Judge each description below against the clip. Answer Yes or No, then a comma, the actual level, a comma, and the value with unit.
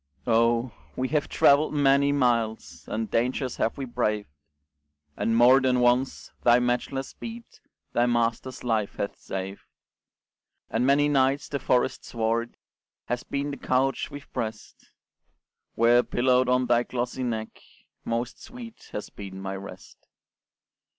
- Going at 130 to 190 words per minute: Yes, slow, 135 wpm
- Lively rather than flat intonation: No, average, 2.7 semitones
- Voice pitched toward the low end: Yes, low, 125 Hz